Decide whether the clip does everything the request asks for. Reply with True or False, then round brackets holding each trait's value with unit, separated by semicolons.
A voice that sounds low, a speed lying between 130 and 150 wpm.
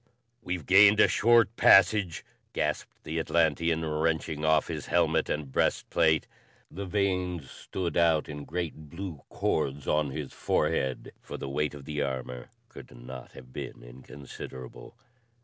True (80 Hz; 145 wpm)